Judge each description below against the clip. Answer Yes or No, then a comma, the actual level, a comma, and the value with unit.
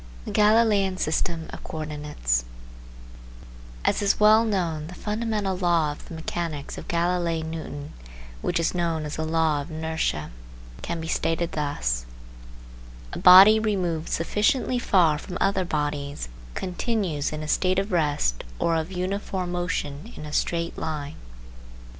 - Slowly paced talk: No, average, 145 wpm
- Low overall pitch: No, medium, 170 Hz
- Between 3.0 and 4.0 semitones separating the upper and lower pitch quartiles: Yes, average, 3.7 semitones